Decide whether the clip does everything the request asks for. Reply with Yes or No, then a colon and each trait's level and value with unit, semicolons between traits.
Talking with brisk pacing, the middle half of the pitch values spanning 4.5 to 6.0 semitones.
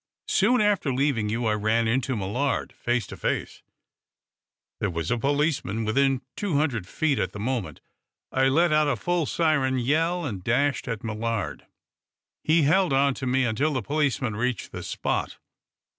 No: average, 165 wpm; average, 4.8 semitones